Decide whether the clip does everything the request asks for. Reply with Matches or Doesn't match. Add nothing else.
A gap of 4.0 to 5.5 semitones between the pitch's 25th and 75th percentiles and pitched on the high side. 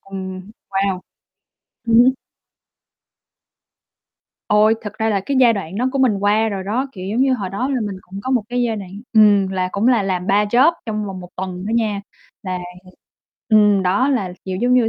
Doesn't match